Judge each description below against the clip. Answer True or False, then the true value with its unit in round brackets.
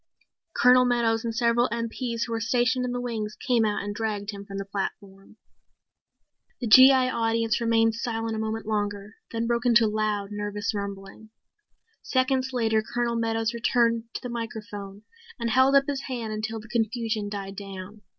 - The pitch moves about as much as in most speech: False (2.2 semitones)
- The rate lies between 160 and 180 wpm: True (170 wpm)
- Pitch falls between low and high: False (225 Hz)